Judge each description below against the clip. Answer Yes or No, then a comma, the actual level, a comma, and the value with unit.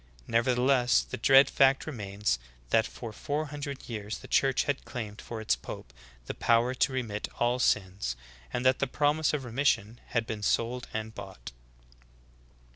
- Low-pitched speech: Yes, low, 120 Hz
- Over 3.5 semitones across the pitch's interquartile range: Yes, average, 3.9 semitones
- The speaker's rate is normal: Yes, average, 165 wpm